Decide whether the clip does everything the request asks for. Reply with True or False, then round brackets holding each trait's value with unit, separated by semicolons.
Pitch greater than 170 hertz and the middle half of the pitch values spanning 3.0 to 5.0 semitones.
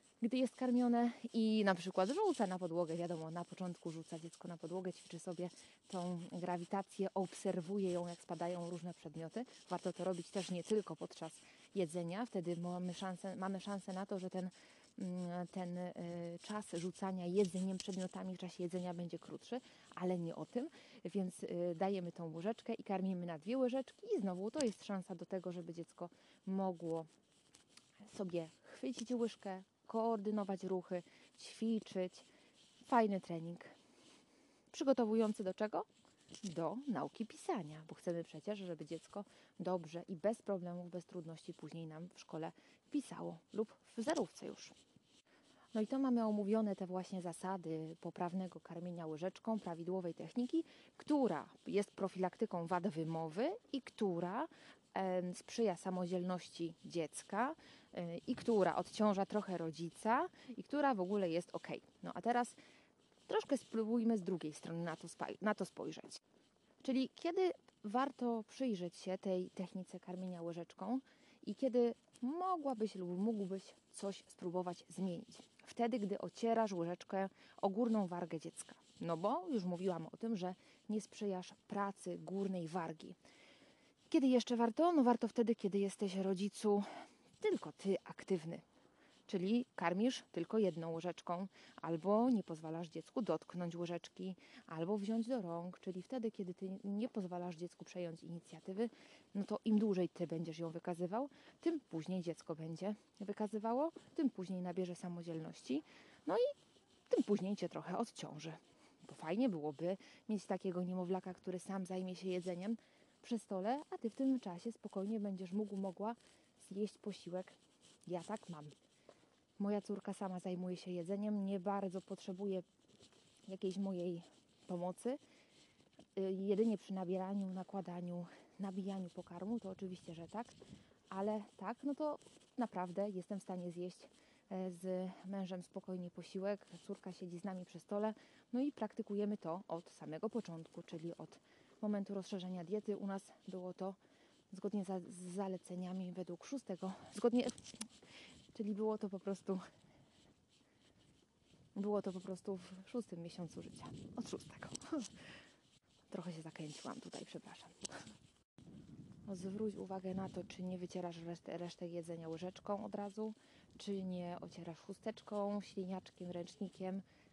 True (190 Hz; 3.8 semitones)